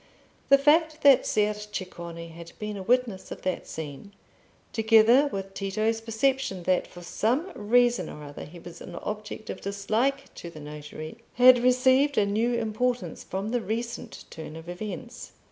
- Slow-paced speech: No, average, 160 wpm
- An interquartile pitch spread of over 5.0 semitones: Yes, wide, 5.4 semitones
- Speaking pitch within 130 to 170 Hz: No, high, 215 Hz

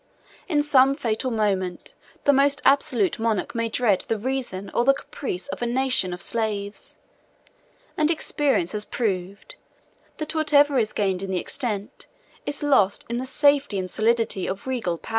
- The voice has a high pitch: Yes, high, 235 Hz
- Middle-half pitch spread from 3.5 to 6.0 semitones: Yes, wide, 5.6 semitones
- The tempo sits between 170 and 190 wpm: No, average, 160 wpm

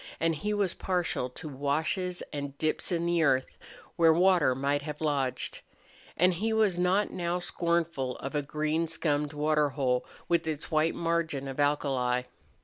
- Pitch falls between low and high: Yes, medium, 155 Hz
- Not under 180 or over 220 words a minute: No, average, 160 wpm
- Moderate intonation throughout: Yes, average, 3.3 semitones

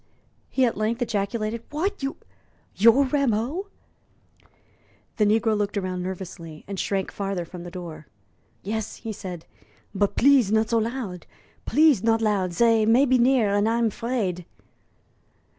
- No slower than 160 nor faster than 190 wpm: No, average, 140 wpm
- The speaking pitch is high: Yes, high, 220 Hz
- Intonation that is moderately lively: Yes, average, 3.6 semitones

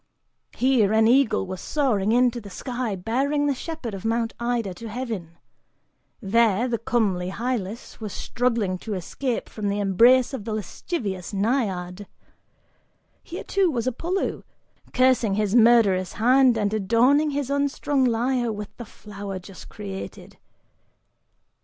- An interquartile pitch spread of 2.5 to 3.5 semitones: No, average, 4.1 semitones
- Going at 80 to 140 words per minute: Yes, slow, 135 wpm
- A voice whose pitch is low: No, high, 230 Hz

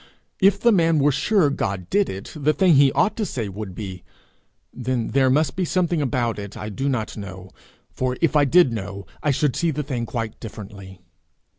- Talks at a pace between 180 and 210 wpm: Yes, average, 200 wpm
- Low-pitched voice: Yes, low, 130 Hz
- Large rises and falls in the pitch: Yes, wide, 6.6 semitones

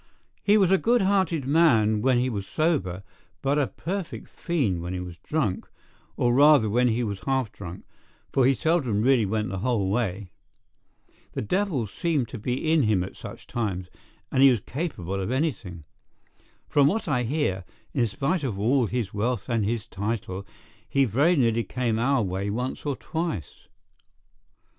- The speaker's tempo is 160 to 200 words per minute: Yes, average, 170 wpm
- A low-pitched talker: Yes, low, 120 Hz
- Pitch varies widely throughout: Yes, wide, 6.2 semitones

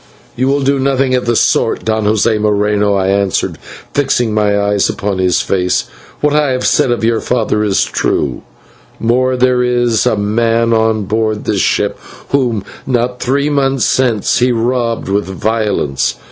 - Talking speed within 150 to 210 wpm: Yes, average, 165 wpm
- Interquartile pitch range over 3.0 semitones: Yes, average, 3.5 semitones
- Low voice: Yes, low, 115 Hz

